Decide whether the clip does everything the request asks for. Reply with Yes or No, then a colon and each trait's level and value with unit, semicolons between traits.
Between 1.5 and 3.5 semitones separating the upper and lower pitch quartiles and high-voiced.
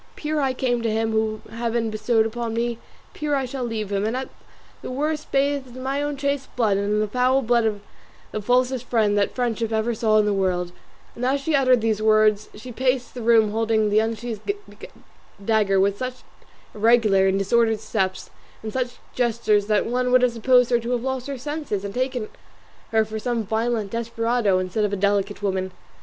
Yes: average, 2.9 semitones; high, 230 Hz